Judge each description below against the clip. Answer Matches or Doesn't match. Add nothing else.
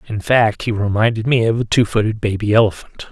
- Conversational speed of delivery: Doesn't match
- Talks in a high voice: Doesn't match